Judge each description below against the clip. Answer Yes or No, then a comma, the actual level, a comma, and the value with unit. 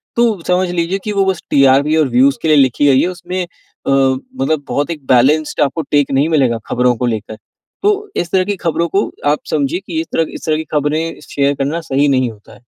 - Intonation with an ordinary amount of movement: Yes, average, 4.2 semitones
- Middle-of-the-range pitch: Yes, medium, 150 Hz